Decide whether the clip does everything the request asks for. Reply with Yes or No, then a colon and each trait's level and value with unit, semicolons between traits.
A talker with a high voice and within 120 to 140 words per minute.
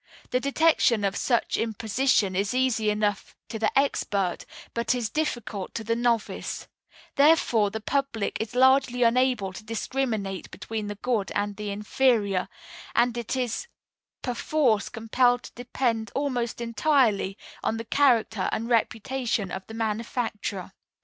Yes: high, 230 Hz; slow, 135 wpm